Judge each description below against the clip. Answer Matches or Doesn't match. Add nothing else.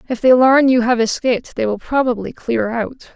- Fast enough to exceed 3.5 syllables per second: Matches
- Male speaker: Doesn't match